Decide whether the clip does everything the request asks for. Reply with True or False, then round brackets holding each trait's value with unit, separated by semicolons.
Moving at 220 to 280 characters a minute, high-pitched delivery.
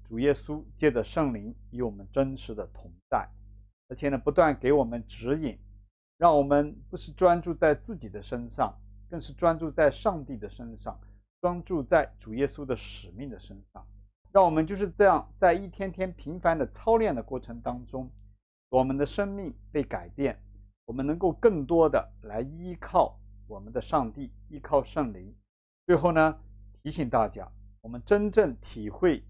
False (250 characters per minute; 130 Hz)